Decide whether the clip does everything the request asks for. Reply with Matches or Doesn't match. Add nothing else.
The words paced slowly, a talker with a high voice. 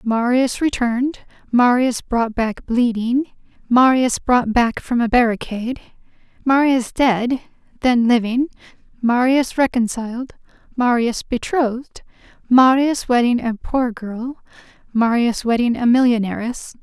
Matches